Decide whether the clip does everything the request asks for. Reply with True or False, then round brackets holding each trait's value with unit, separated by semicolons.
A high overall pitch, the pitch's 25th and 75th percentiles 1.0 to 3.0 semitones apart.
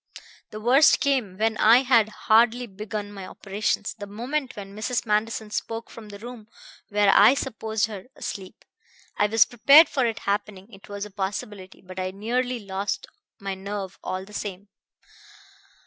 True (210 Hz; 2.5 semitones)